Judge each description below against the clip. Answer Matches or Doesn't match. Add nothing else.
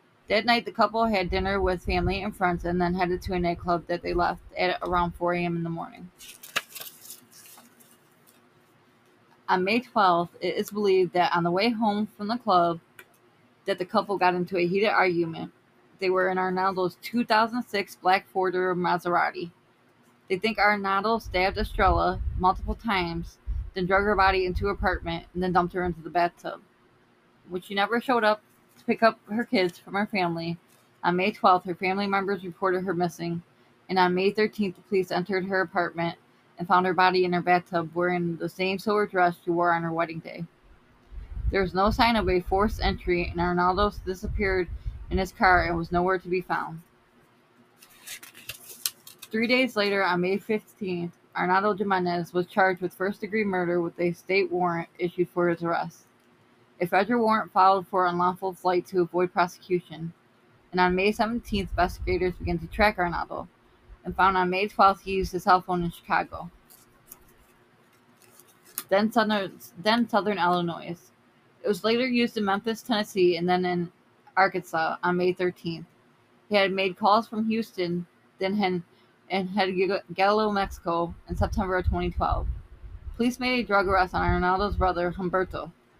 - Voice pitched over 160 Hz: Matches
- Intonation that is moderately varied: Doesn't match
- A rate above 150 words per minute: Matches